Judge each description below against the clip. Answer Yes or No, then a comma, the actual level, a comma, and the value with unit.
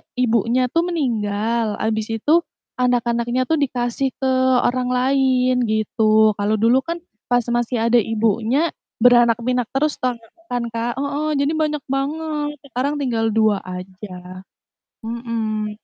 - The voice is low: No, high, 240 Hz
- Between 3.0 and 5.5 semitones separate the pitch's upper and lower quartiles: Yes, average, 3.3 semitones